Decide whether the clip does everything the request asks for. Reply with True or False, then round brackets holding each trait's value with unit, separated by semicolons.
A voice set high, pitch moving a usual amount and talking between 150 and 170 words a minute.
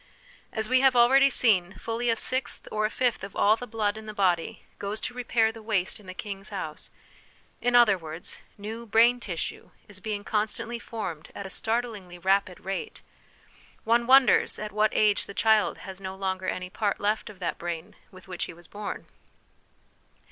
False (210 Hz; 3.3 semitones; 185 wpm)